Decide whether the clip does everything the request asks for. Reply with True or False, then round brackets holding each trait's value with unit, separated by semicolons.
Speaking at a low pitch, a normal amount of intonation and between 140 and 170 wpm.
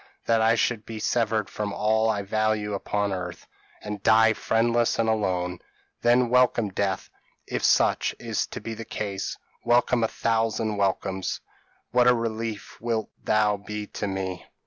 False (110 Hz; 2.0 semitones; 155 wpm)